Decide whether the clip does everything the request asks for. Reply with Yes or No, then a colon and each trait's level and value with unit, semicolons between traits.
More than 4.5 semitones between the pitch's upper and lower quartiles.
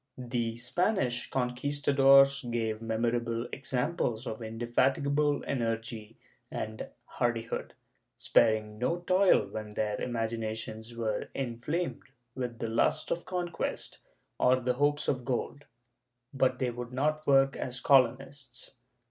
No: average, 3.2 semitones